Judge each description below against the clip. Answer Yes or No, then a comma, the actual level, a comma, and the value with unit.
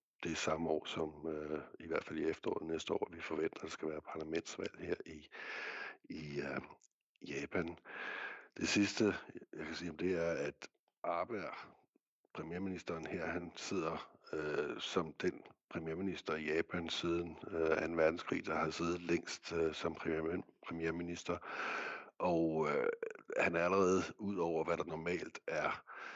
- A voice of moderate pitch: No, very low, 80 Hz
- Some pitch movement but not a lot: No, narrow, 2.1 semitones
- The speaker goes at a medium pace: Yes, average, 155 wpm